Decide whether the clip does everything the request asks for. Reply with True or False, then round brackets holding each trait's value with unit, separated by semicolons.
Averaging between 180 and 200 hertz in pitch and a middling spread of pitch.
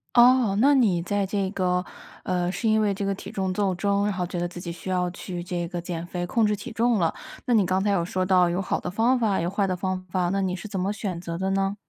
False (190 Hz; 2.3 semitones)